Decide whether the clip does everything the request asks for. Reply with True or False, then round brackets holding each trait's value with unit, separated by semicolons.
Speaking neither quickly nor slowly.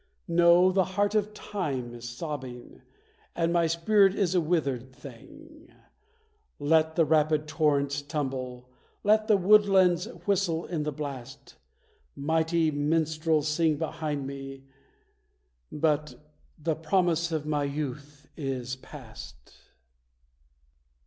False (110 wpm)